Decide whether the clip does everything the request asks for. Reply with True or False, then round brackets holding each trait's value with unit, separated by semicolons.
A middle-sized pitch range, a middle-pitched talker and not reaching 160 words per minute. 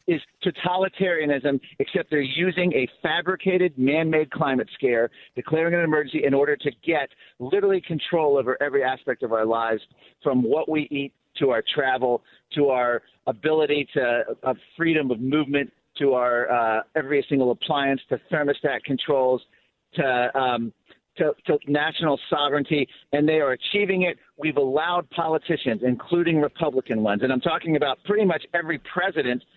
True (4.4 semitones; 145 Hz; 150 wpm)